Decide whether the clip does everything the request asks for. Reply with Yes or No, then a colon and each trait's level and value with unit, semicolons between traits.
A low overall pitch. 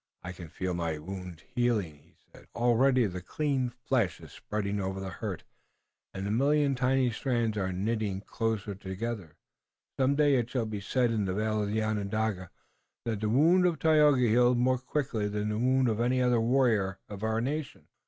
Yes: low, 110 Hz